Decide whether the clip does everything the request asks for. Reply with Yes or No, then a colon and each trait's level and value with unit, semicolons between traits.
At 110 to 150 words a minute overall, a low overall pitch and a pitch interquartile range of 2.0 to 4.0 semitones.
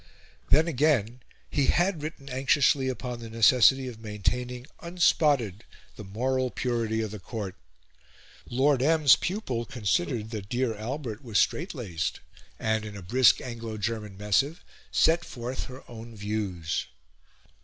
Yes: slow, 135 wpm; low, 120 Hz; average, 3.7 semitones